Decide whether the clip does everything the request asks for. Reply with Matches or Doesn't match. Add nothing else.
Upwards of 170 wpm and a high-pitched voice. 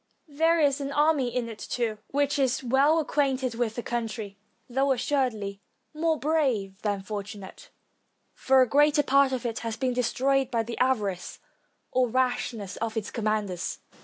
Doesn't match